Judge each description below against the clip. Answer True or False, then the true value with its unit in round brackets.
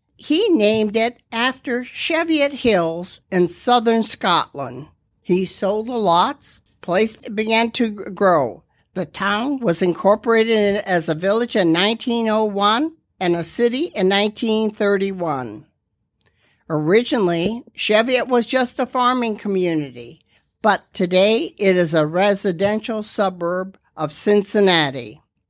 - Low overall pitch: False (205 Hz)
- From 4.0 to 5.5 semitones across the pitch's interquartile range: True (4.4 semitones)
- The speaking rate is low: True (110 wpm)